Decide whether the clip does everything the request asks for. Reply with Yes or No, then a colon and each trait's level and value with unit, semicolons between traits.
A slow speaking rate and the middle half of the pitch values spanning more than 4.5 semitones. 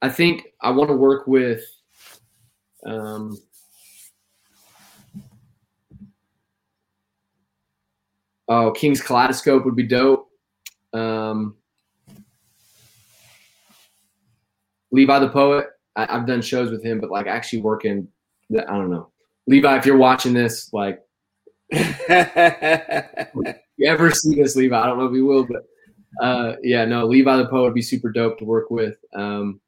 No: slow, 125 wpm; average, 4.0 semitones